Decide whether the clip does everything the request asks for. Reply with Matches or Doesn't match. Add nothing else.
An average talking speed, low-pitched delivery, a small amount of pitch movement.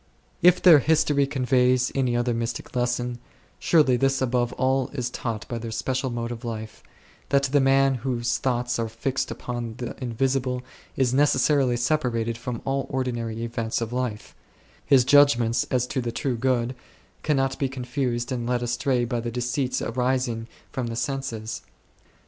Matches